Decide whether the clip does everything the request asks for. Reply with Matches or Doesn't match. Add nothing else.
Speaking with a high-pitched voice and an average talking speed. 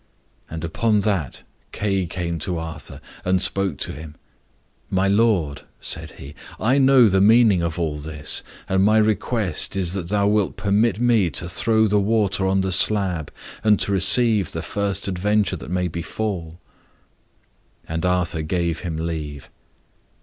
Doesn't match